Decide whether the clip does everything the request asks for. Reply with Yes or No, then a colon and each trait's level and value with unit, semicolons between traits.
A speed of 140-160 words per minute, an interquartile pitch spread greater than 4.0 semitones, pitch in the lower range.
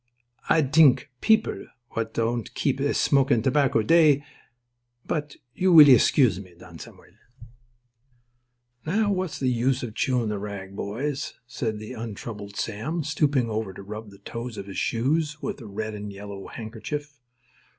Yes: average, 145 wpm; average, 5.3 semitones; low, 120 Hz